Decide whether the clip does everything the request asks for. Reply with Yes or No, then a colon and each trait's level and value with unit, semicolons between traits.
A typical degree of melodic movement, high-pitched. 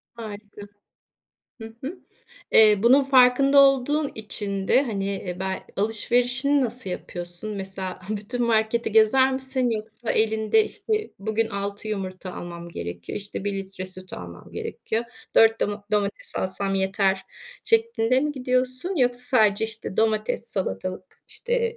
Yes: average, 4.4 semitones; high, 220 Hz